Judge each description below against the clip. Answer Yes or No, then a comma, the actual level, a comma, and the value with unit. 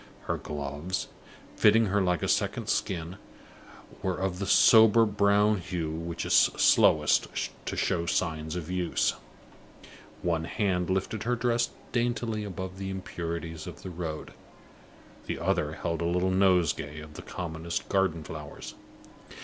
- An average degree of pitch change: Yes, average, 3.5 semitones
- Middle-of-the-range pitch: No, very low, 90 Hz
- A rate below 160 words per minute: Yes, average, 140 wpm